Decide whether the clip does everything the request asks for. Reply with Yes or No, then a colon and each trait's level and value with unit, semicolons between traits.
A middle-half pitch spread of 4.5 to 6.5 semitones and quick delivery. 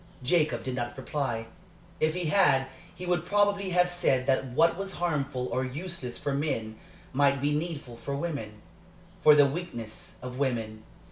No: average, 5.3 semitones; average, 160 wpm